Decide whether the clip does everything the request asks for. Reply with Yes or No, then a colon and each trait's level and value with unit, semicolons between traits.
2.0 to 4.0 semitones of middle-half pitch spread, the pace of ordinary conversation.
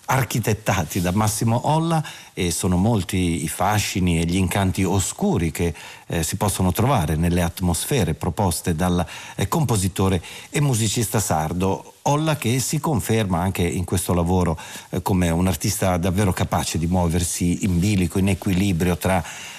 Yes: average, 3.5 semitones; average, 145 wpm